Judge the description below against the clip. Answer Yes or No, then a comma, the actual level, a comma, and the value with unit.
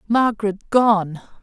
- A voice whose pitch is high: Yes, high, 210 Hz